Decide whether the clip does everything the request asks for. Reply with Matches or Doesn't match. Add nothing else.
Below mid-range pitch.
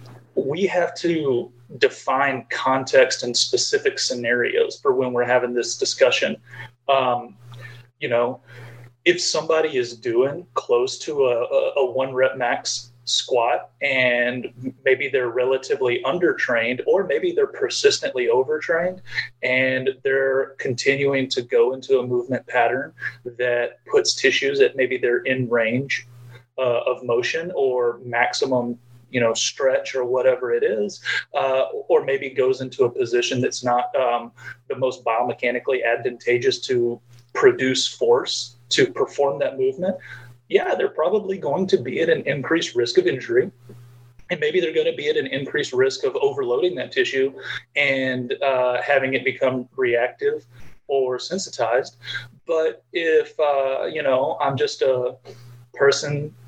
Doesn't match